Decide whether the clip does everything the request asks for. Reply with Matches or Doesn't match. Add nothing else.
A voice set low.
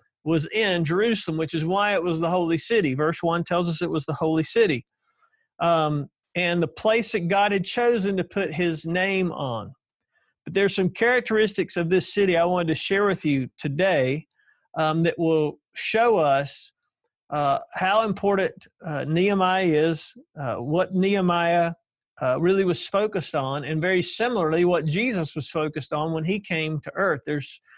Doesn't match